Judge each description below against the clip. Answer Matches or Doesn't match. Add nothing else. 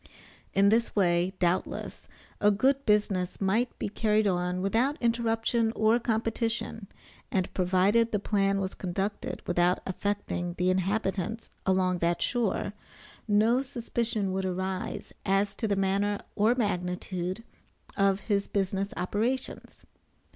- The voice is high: Matches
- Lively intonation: Doesn't match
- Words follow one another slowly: Matches